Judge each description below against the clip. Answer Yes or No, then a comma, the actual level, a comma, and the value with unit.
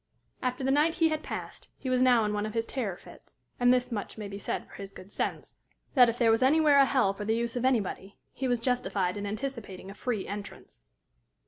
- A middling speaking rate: No, fast, 235 wpm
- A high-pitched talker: Yes, high, 235 Hz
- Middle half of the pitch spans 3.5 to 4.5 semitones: Yes, average, 4.1 semitones